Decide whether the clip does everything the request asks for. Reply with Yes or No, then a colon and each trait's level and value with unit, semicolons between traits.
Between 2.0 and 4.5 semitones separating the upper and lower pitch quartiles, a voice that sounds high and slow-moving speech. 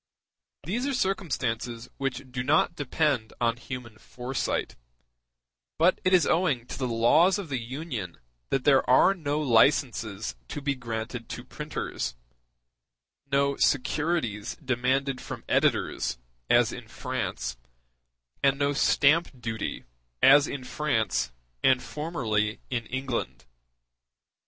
No: average, 4.2 semitones; low, 130 Hz; slow, 120 wpm